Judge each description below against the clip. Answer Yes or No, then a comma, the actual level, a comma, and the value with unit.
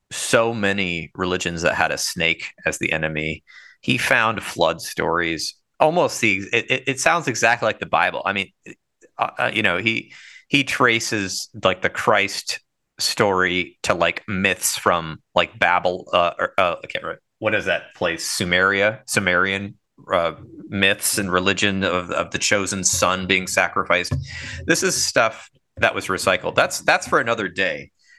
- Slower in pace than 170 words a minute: Yes, average, 160 wpm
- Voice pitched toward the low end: Yes, low, 100 Hz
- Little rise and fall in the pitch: No, average, 3.2 semitones